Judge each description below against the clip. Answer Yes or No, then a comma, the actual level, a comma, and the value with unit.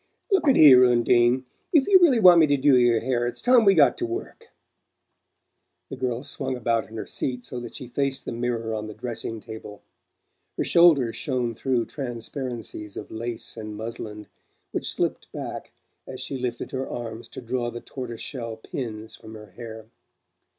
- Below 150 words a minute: No, average, 180 wpm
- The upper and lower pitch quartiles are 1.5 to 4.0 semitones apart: Yes, average, 3.0 semitones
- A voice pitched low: Yes, low, 120 Hz